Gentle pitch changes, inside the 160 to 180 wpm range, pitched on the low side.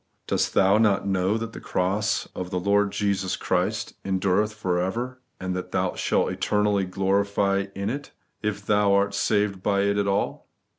Yes: narrow, 1.4 semitones; average, 170 wpm; low, 100 Hz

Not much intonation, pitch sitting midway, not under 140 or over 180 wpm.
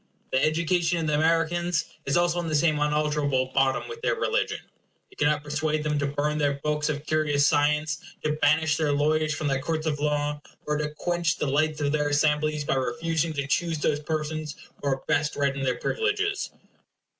No: narrow, 1.5 semitones; medium, 150 Hz; average, 195 wpm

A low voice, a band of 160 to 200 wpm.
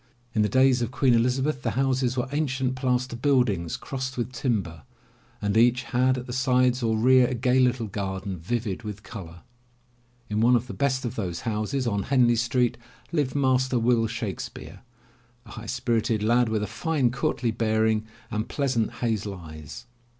Yes: low, 120 Hz; average, 170 wpm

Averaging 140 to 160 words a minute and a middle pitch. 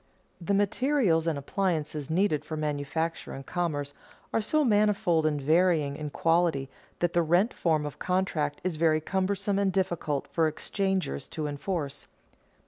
Yes: average, 150 wpm; medium, 165 Hz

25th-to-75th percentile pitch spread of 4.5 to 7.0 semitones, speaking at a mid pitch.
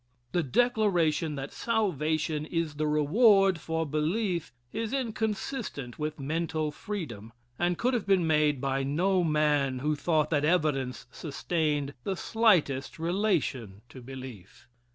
Yes: average, 4.9 semitones; medium, 155 Hz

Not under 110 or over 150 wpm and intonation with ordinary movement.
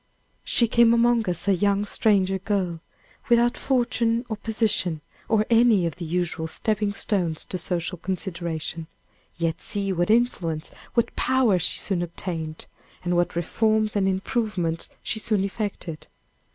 Yes: average, 140 wpm; average, 4.3 semitones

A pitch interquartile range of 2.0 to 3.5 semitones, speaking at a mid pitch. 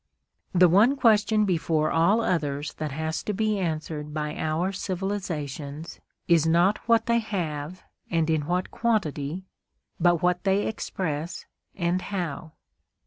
No: average, 4.2 semitones; medium, 175 Hz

